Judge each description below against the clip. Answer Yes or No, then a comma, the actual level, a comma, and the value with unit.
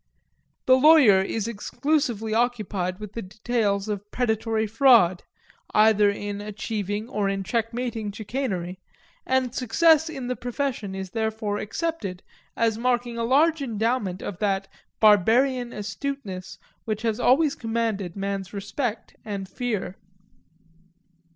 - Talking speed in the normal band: No, slow, 120 wpm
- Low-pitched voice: No, high, 220 Hz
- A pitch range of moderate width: Yes, average, 3.6 semitones